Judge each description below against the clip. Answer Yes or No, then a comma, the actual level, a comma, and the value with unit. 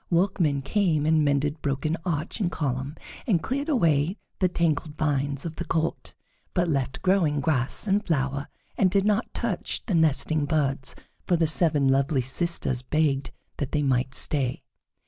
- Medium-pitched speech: Yes, medium, 155 Hz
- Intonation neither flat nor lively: Yes, average, 3.7 semitones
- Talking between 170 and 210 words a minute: No, average, 160 wpm